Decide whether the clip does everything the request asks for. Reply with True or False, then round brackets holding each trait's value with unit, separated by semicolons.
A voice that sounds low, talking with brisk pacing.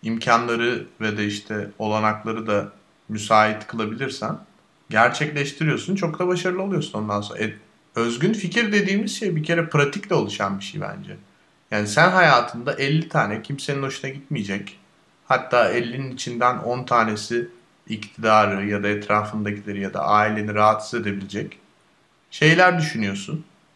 False (115 Hz; 130 wpm)